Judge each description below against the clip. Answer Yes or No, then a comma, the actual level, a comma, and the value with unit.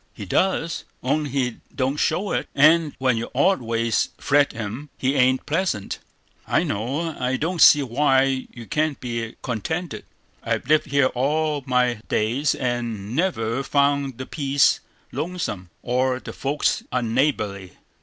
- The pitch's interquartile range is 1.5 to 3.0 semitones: No, average, 3.8 semitones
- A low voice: Yes, low, 130 Hz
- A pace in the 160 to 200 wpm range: No, average, 145 wpm